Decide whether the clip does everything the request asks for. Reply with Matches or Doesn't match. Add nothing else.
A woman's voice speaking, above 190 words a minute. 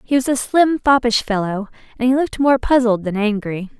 Matches